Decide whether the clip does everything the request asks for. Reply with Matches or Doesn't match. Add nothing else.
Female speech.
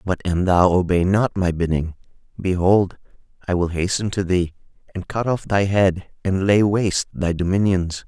Doesn't match